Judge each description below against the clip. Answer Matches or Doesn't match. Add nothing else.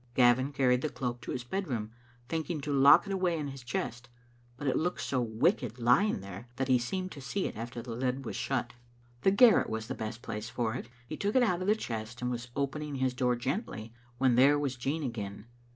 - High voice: Doesn't match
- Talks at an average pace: Doesn't match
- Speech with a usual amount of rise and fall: Matches